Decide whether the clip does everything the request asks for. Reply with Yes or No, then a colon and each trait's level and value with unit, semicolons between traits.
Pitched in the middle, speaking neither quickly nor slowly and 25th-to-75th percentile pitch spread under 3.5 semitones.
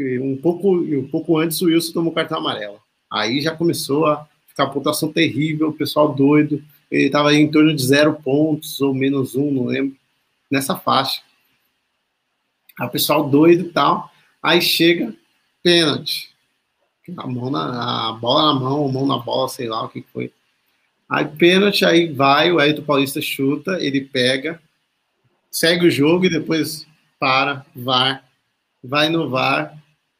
Yes: medium, 150 Hz; average, 160 wpm; average, 2.8 semitones